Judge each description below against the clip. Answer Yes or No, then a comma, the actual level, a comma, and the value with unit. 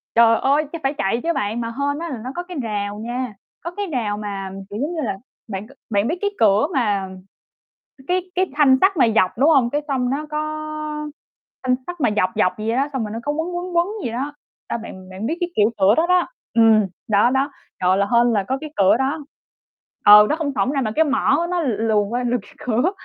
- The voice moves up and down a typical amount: No, wide, 6.2 semitones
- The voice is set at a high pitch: Yes, very high, 250 Hz